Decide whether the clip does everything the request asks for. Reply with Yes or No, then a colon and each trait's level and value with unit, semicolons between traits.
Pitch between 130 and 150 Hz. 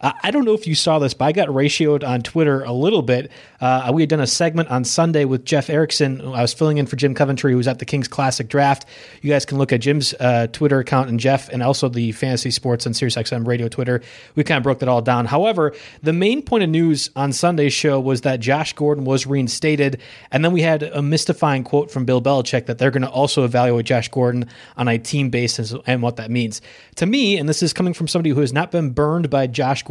Yes: medium, 140 Hz